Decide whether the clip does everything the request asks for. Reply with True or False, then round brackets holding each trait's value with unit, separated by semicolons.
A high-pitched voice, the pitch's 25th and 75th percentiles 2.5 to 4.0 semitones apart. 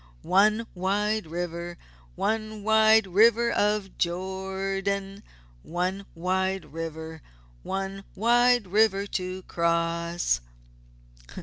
True (195 Hz; 3.3 semitones)